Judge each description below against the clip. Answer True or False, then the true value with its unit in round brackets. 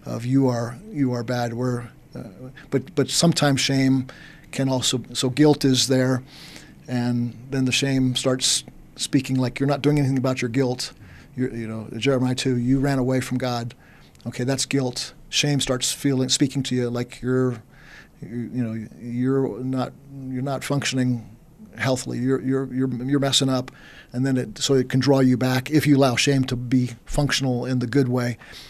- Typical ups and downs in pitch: False (1.6 semitones)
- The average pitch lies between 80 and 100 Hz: False (130 Hz)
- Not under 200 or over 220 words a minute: False (185 wpm)